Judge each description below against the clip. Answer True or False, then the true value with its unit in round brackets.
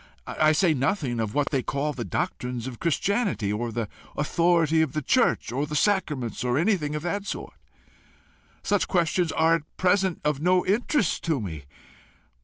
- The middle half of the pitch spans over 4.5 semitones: True (5.5 semitones)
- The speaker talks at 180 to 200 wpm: False (170 wpm)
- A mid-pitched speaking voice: True (155 Hz)